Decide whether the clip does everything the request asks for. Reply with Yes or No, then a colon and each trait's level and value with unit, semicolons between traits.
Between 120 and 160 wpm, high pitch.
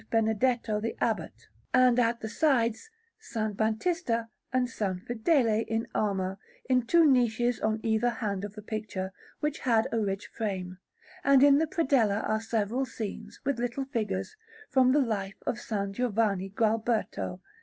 Yes: average, 155 wpm; high, 225 Hz